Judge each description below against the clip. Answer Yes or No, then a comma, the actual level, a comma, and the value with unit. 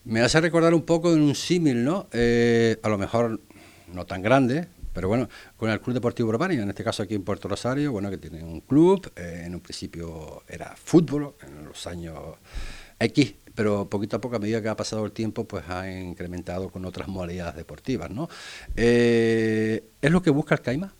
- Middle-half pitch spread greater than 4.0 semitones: Yes, average, 5.1 semitones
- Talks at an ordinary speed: No, fast, 205 wpm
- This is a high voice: No, low, 110 Hz